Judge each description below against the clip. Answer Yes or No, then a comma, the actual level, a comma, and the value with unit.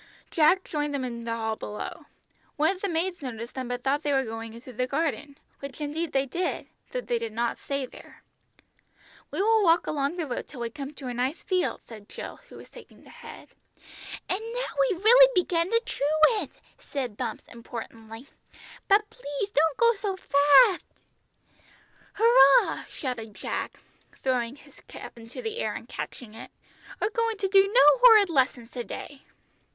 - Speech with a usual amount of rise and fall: No, wide, 7.6 semitones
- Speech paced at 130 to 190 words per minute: Yes, average, 180 wpm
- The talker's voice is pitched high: Yes, very high, 285 Hz